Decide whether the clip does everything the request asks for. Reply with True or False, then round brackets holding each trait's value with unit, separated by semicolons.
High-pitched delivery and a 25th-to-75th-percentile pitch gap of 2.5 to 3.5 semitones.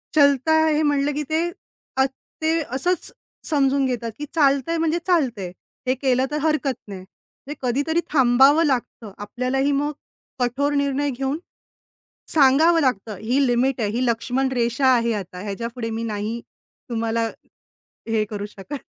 False (265 Hz; 3.9 semitones)